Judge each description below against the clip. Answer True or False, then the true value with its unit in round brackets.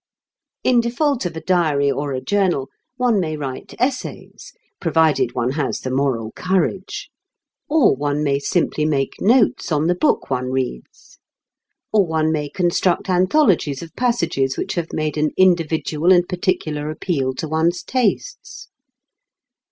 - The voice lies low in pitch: False (160 Hz)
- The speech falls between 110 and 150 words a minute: True (145 wpm)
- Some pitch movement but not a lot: True (4.7 semitones)